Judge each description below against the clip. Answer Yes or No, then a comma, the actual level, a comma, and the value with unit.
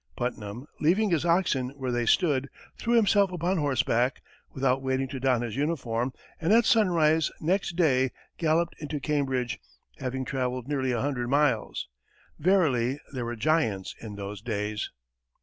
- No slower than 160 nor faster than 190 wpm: No, average, 150 wpm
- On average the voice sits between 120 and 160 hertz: Yes, low, 135 Hz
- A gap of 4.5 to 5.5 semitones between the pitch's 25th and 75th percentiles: Yes, average, 4.9 semitones